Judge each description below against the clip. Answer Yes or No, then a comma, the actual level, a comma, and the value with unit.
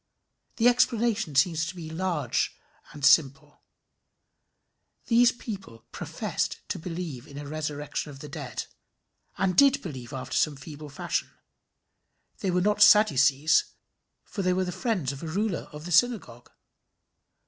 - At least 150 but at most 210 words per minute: No, average, 140 wpm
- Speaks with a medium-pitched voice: Yes, medium, 160 Hz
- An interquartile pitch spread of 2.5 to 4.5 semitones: No, wide, 5.4 semitones